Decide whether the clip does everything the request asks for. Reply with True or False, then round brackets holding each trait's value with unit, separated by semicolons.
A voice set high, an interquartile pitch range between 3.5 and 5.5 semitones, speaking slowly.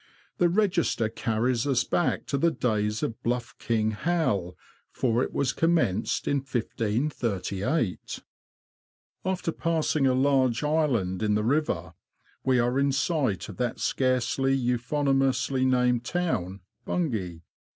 False (125 Hz; 4.5 semitones; 130 wpm)